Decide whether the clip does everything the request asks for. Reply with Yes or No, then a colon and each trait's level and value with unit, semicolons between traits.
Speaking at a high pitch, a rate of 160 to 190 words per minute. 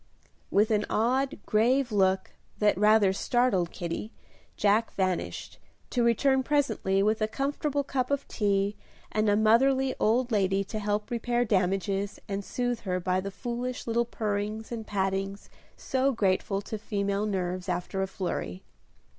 No: high, 210 Hz; average, 145 wpm